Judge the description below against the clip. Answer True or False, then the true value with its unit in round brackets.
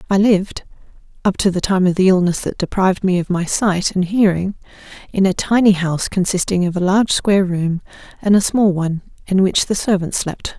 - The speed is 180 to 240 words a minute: True (205 wpm)